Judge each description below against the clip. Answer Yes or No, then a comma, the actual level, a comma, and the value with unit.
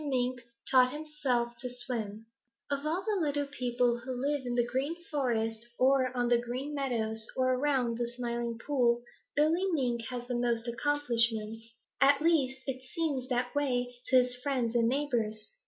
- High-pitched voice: Yes, very high, 250 Hz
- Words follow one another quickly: No, average, 165 wpm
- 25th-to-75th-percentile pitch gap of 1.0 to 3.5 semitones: Yes, average, 2.9 semitones